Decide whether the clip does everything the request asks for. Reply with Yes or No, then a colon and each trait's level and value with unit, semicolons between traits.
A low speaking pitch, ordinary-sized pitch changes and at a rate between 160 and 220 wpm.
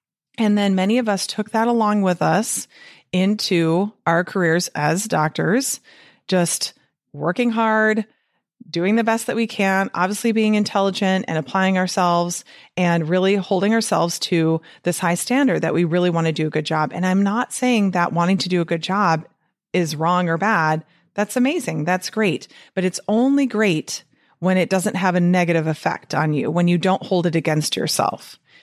No: medium, 185 Hz; average, 3.7 semitones; average, 180 wpm